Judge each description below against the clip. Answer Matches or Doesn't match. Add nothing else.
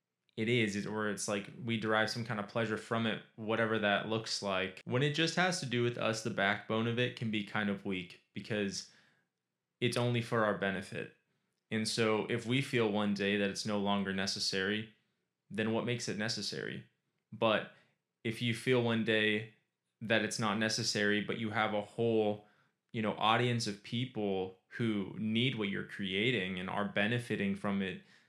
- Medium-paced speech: Matches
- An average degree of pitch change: Doesn't match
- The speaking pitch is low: Matches